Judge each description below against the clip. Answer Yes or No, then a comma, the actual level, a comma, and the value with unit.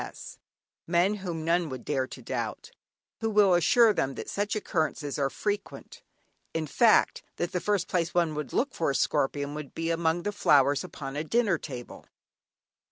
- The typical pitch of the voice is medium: Yes, medium, 165 Hz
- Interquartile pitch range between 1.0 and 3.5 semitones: No, wide, 5.4 semitones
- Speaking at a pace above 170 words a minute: Yes, average, 180 wpm